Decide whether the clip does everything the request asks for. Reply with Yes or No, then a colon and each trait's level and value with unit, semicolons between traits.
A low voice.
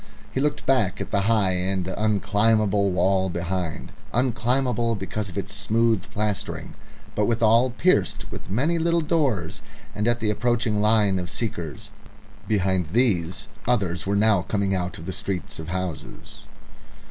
Yes: low, 105 Hz